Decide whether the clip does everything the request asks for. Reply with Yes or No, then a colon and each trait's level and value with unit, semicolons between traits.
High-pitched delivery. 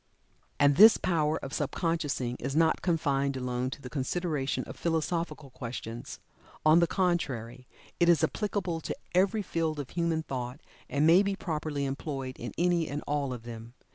No: medium, 150 Hz